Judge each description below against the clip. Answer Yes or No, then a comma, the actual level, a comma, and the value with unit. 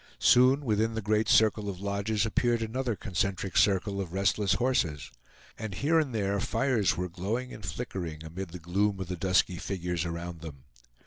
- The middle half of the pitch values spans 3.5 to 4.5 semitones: Yes, average, 3.9 semitones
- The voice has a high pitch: No, low, 100 Hz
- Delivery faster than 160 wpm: Yes, average, 175 wpm